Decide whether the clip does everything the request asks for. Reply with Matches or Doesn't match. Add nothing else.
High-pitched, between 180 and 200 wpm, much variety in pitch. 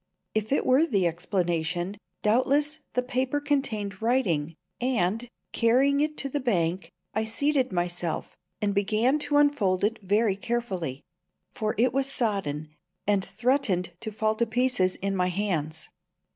Doesn't match